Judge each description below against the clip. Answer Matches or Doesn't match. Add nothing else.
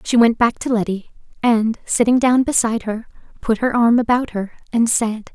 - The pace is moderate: Matches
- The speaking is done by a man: Doesn't match